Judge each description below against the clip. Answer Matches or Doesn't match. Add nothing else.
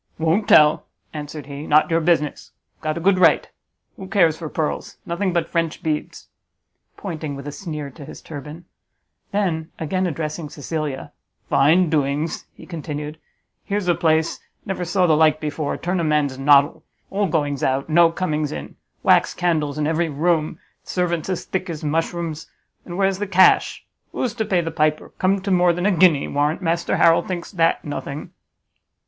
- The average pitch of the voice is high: Doesn't match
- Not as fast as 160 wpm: Doesn't match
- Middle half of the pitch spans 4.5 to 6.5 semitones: Doesn't match